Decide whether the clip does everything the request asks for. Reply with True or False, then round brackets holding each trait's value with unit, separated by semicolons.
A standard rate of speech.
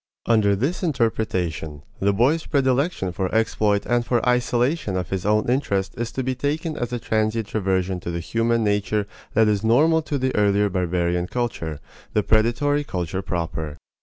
True (165 wpm)